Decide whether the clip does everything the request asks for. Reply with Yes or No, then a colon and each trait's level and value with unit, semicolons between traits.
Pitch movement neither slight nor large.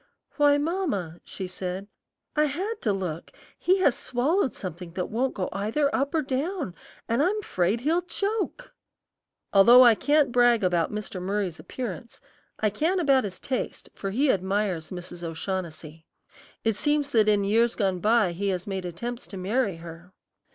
No: wide, 7.3 semitones